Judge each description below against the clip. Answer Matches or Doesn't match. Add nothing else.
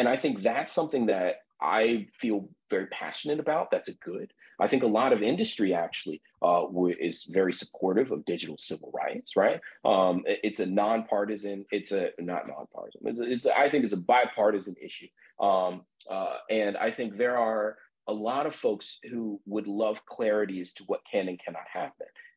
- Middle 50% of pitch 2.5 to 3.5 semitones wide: Matches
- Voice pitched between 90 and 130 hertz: Matches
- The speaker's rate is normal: Matches